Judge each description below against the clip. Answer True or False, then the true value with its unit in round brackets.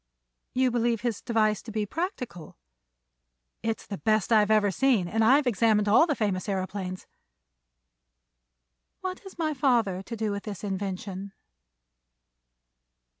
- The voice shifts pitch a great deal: False (3.5 semitones)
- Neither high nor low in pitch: False (215 Hz)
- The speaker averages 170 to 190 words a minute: False (135 wpm)